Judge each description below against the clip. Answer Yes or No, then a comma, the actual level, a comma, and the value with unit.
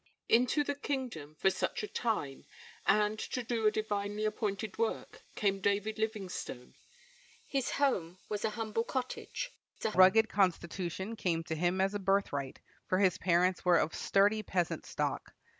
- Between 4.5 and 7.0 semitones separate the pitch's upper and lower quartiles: No, average, 3.3 semitones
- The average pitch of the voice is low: No, high, 205 Hz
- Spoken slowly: No, average, 155 wpm